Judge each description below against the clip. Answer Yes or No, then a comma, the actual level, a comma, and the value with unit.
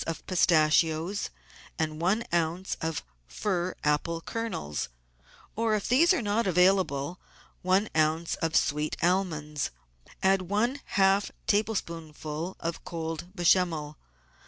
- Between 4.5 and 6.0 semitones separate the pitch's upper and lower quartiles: No, average, 3.7 semitones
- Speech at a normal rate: No, slow, 115 wpm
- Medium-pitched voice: Yes, medium, 175 Hz